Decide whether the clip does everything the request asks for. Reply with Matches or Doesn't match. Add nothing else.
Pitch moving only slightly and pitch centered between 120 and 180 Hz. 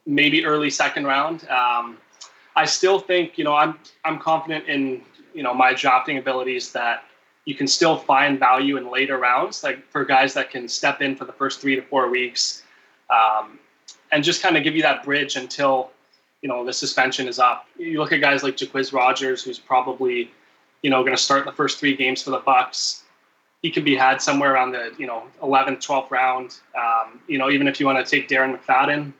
Matches